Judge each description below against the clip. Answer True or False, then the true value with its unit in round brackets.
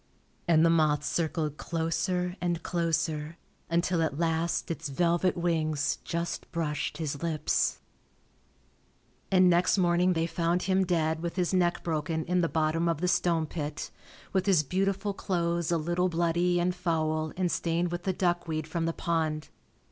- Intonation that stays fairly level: True (1.8 semitones)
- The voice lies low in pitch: False (170 Hz)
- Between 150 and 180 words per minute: True (155 wpm)